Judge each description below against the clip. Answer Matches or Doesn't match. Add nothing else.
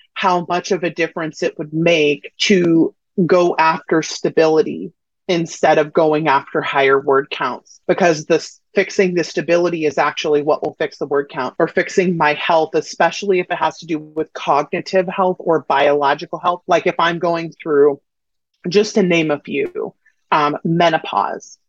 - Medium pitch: Matches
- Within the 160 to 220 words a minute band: Matches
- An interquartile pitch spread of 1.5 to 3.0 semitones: Matches